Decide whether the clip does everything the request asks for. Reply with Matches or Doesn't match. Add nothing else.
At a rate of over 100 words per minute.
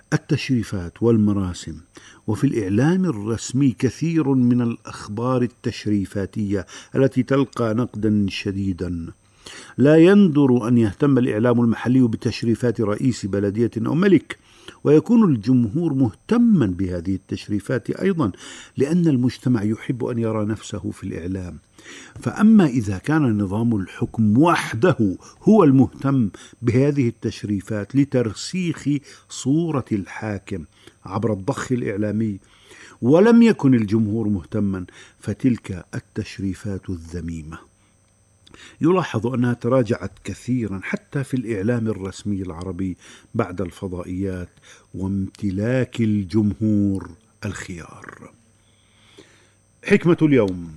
Doesn't match